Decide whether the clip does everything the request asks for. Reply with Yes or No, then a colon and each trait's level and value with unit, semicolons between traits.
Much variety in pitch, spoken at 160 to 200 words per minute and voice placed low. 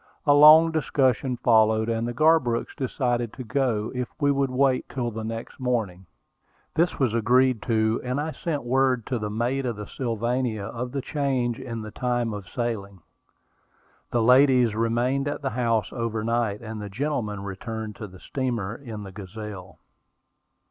No: average, 3.1 semitones; average, 165 wpm; low, 120 Hz